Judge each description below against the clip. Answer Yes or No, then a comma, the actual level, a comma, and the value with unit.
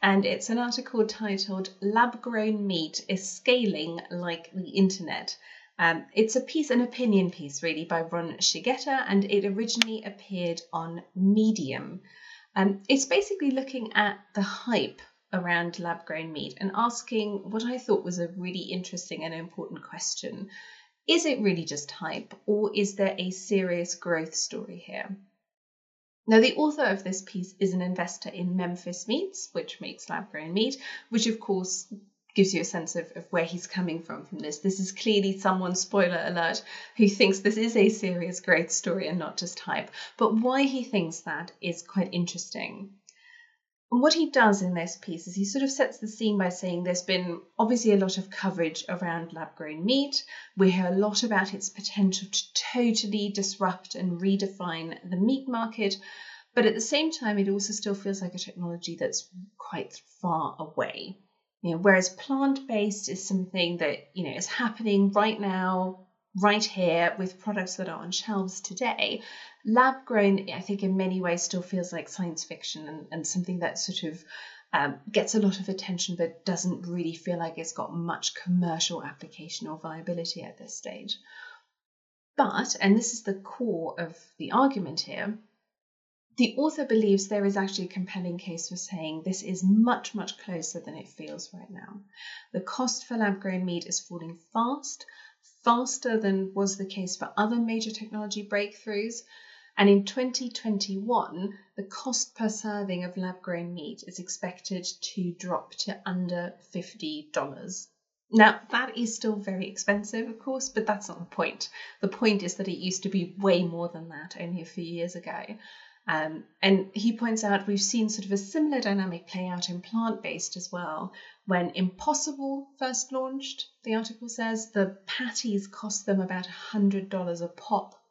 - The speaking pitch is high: Yes, high, 195 Hz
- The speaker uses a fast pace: No, average, 175 wpm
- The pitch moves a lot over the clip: No, average, 3.8 semitones